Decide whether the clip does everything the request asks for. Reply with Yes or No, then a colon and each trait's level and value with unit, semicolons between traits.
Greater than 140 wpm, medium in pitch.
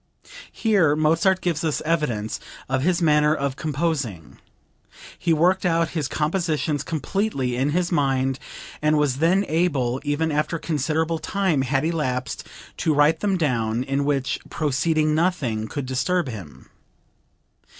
No: slow, 135 wpm; medium, 150 Hz